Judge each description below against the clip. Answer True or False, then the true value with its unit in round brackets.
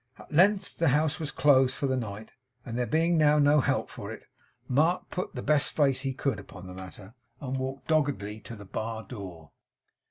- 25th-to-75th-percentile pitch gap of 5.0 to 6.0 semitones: True (5.4 semitones)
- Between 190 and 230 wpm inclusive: True (200 wpm)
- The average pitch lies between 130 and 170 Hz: True (135 Hz)